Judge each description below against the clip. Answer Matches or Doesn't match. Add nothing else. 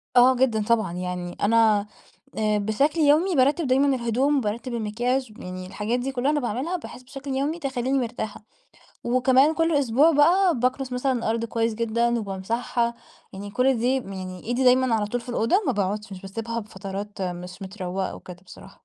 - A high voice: Matches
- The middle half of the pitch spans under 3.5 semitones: Doesn't match